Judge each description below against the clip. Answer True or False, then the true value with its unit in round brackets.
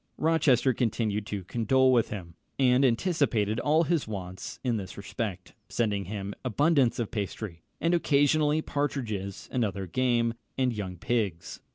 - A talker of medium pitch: False (115 Hz)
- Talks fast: False (145 wpm)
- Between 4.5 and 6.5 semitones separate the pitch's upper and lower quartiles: True (5.1 semitones)